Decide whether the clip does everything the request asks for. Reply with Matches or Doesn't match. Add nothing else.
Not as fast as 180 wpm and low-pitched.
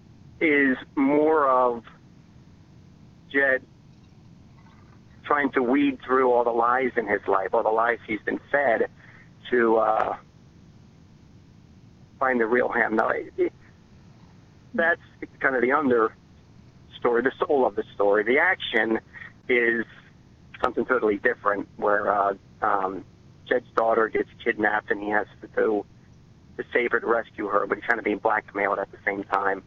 Matches